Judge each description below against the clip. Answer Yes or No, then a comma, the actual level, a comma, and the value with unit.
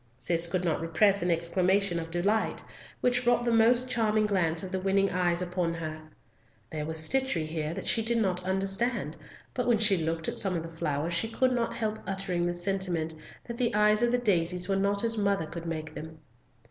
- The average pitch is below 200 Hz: Yes, high, 190 Hz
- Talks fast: Yes, fast, 210 wpm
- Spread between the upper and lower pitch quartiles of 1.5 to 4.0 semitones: No, average, 4.6 semitones